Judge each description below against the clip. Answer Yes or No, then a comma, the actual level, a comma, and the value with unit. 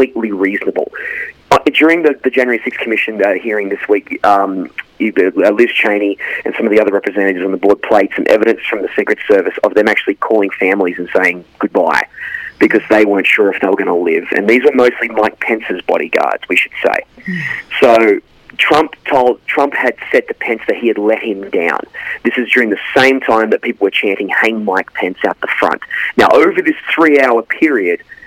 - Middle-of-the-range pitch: No, low, 120 Hz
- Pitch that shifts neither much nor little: No, wide, 8.6 semitones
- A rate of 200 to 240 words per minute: Yes, fast, 205 wpm